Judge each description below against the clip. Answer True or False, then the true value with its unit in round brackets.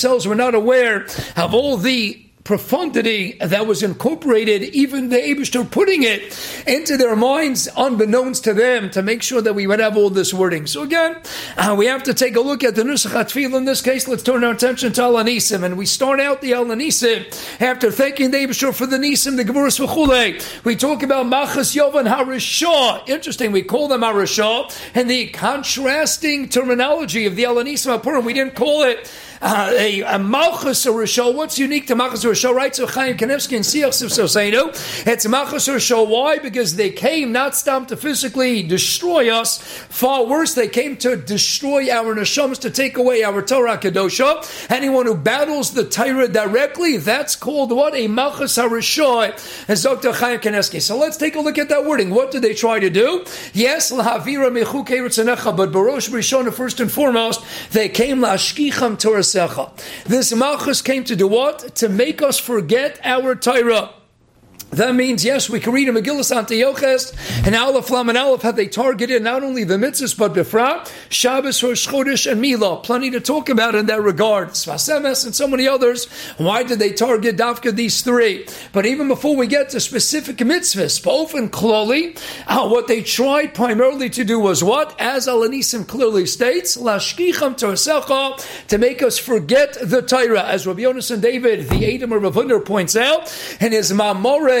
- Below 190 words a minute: True (175 wpm)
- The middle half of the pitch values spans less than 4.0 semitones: True (3.3 semitones)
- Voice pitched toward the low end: False (245 Hz)